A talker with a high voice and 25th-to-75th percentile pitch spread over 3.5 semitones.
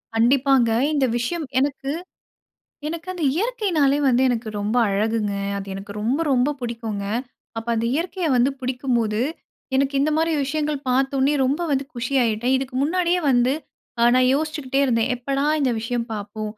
Yes: very high, 260 Hz; average, 3.9 semitones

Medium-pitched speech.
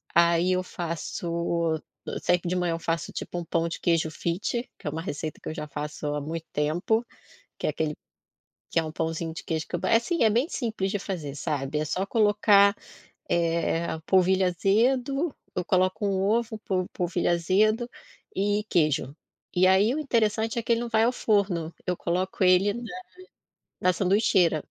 Yes: medium, 180 Hz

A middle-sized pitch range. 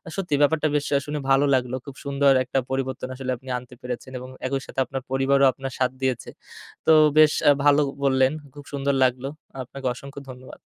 No: narrow, 1.5 semitones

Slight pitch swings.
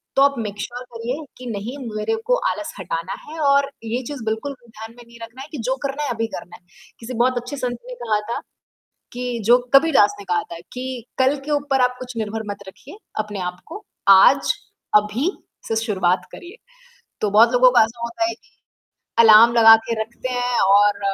No: average, 3.3 semitones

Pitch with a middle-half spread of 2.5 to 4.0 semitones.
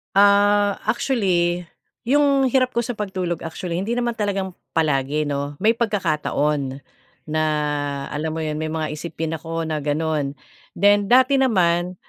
No: average, 5.1 semitones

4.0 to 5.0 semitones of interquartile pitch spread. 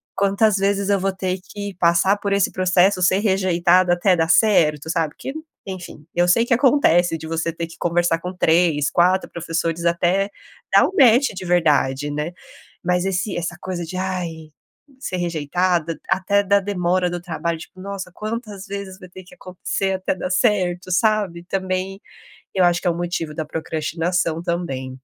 No: narrow, 2.4 semitones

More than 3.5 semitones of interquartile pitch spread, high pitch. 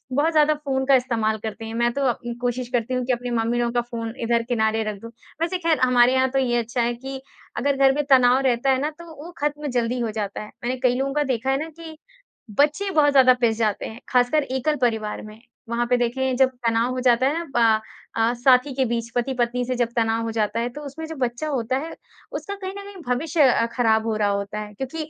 No: average, 2.9 semitones; high, 245 Hz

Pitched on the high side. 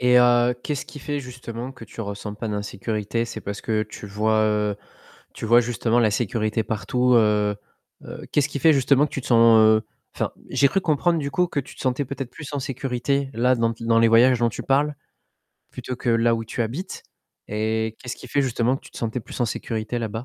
No: low, 120 Hz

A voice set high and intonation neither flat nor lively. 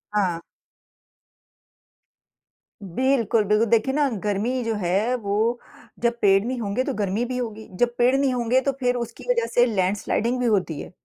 Yes: high, 230 Hz; average, 3.5 semitones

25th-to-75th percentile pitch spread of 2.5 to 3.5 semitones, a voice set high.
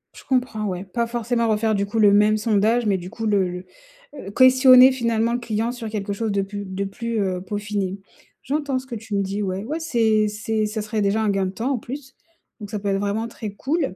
Yes: average, 2.8 semitones; high, 215 Hz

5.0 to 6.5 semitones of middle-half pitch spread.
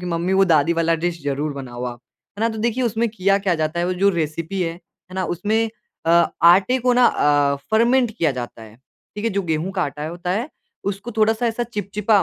Yes: wide, 5.5 semitones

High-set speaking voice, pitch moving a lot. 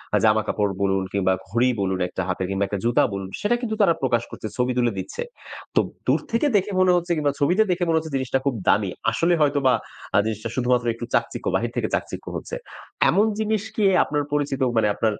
No: low, 125 Hz; wide, 7.8 semitones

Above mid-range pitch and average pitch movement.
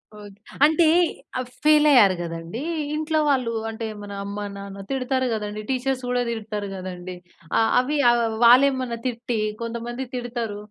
Yes: high, 235 Hz; average, 3.9 semitones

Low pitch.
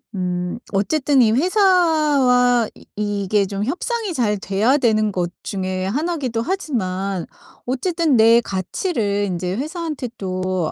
No: high, 225 Hz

